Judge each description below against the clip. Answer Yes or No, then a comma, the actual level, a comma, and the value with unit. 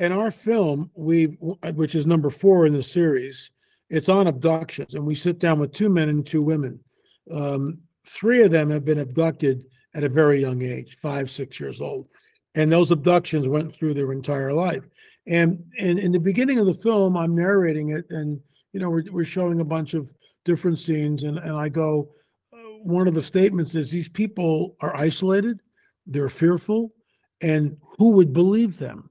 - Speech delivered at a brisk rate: No, average, 185 wpm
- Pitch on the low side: No, medium, 165 Hz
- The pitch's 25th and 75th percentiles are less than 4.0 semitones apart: Yes, average, 3.4 semitones